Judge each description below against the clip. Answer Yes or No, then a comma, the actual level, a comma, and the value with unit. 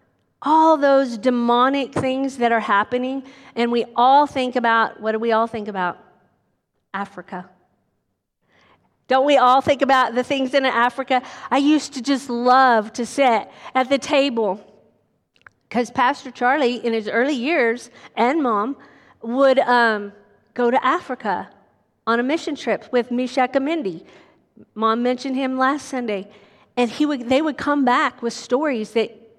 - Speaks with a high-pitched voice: Yes, very high, 250 Hz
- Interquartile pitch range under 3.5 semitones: Yes, average, 2.9 semitones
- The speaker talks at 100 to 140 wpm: No, average, 150 wpm